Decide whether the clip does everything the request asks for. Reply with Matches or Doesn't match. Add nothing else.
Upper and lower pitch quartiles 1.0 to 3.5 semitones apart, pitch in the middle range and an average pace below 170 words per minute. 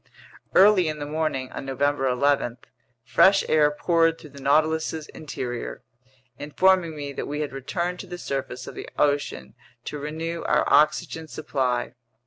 Matches